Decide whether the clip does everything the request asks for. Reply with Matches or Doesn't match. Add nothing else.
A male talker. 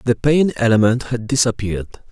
Matches